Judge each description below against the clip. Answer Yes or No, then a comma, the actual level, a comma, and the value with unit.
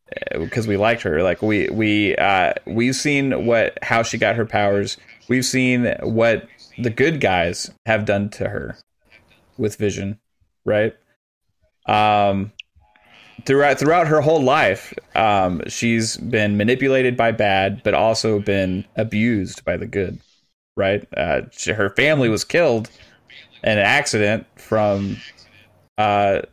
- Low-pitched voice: Yes, low, 110 Hz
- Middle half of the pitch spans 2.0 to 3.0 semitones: Yes, average, 2.7 semitones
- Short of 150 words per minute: Yes, slow, 135 wpm